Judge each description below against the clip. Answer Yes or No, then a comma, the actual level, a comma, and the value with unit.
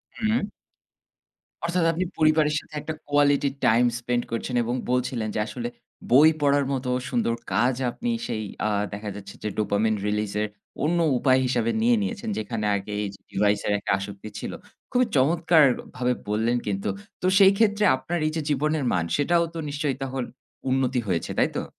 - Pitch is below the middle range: Yes, low, 130 Hz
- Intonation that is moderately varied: No, wide, 6.4 semitones